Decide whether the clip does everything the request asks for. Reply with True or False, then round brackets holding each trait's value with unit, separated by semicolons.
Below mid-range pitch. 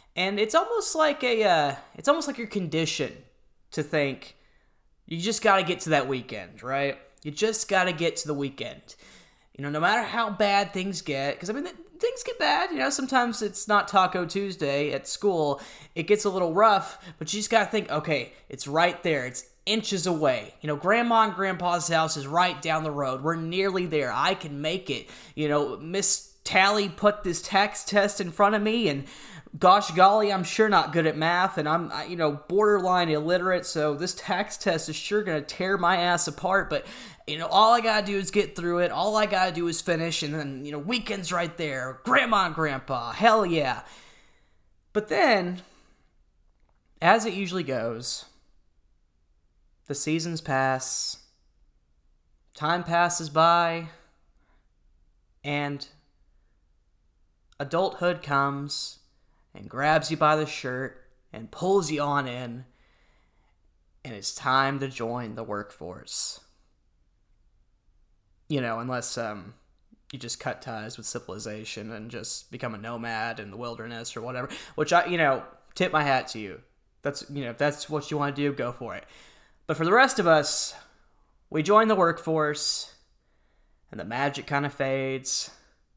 False (155 Hz)